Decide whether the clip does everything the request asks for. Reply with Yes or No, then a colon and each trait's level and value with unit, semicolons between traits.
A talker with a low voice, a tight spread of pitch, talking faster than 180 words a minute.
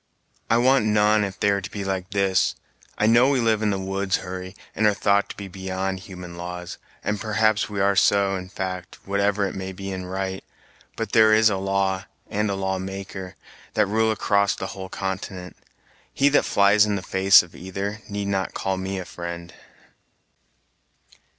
Yes: very low, 95 Hz; narrow, 1.7 semitones; average, 190 wpm